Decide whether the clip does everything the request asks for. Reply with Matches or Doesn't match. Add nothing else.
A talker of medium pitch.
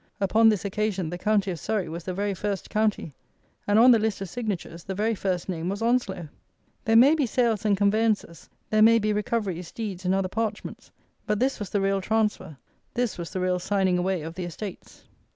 Doesn't match